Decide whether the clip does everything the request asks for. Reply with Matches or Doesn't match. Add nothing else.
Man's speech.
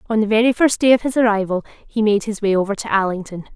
Doesn't match